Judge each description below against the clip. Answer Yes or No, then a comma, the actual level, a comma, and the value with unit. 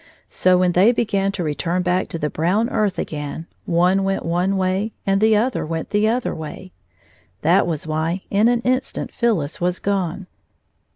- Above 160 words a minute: Yes, average, 175 wpm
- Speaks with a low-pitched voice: No, medium, 185 Hz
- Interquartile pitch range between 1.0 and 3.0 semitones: No, average, 3.7 semitones